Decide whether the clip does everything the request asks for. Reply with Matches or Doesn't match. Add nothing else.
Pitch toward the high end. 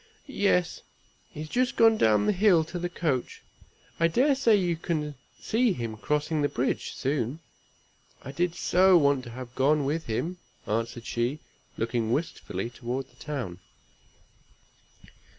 Doesn't match